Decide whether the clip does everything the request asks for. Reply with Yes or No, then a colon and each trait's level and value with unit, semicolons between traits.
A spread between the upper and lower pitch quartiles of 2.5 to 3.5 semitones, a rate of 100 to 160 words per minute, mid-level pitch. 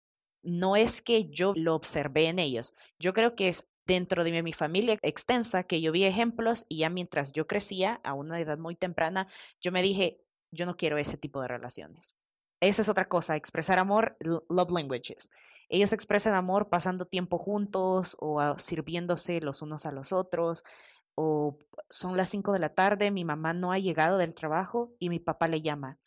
No: average, 3.2 semitones; fast, 190 wpm; medium, 175 Hz